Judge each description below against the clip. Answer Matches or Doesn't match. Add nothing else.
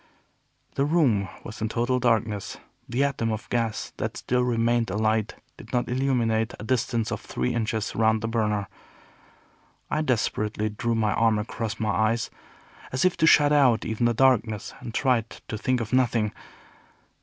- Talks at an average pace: Matches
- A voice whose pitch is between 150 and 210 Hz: Doesn't match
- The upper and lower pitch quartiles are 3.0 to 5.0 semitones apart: Doesn't match